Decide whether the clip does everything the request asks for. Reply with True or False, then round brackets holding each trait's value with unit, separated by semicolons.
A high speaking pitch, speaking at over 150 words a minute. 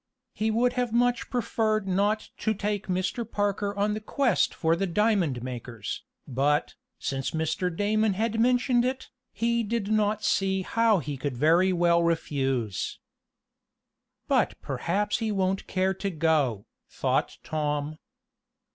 False (195 Hz; 140 wpm)